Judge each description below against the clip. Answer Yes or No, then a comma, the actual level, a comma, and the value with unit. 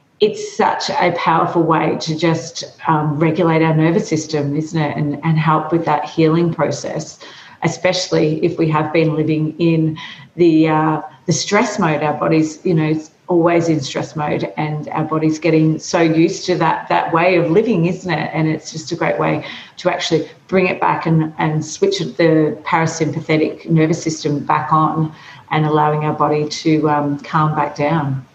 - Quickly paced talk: No, average, 180 wpm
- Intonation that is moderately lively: No, narrow, 1.6 semitones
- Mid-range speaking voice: Yes, medium, 160 Hz